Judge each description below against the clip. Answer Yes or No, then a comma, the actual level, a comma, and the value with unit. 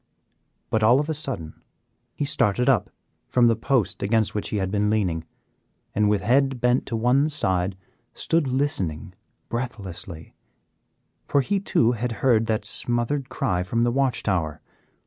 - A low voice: Yes, low, 115 Hz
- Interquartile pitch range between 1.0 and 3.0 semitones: No, average, 4.7 semitones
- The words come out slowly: No, average, 155 wpm